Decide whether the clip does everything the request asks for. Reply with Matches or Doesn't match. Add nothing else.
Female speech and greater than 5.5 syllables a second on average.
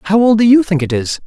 Doesn't match